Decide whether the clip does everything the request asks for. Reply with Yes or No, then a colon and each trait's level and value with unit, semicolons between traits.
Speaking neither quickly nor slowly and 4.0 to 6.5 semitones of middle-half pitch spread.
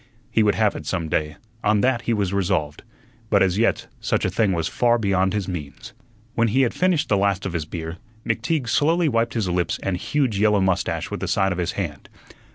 No: fast, 220 wpm; average, 4.4 semitones